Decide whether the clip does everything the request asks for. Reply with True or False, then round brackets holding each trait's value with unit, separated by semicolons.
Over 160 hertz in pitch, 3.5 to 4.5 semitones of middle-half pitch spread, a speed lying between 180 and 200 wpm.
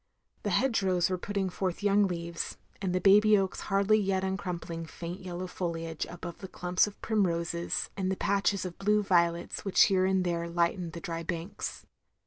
False (185 Hz; 2.5 semitones; 185 wpm)